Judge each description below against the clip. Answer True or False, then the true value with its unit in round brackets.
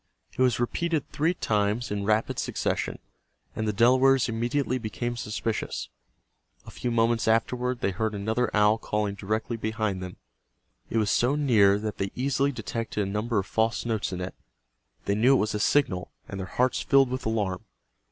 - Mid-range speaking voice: False (110 Hz)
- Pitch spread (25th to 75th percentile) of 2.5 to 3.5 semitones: True (3.0 semitones)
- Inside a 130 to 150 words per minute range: False (175 wpm)